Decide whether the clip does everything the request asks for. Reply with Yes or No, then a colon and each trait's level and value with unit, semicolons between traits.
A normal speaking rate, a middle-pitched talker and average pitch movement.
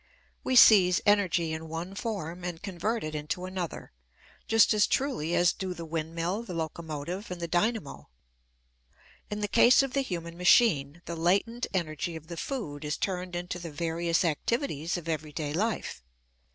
Yes: average, 165 wpm; medium, 175 Hz; average, 4.0 semitones